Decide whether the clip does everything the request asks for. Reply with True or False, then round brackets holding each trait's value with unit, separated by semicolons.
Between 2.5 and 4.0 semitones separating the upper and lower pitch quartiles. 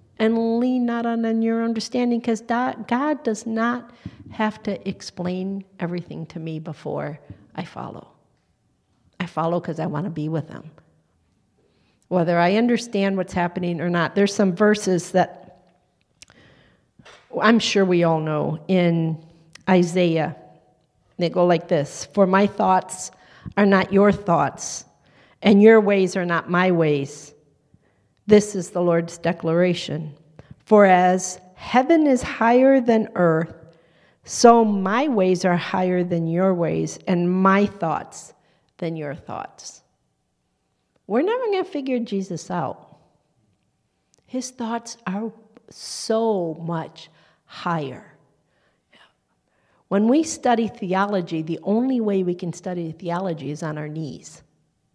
False (4.7 semitones)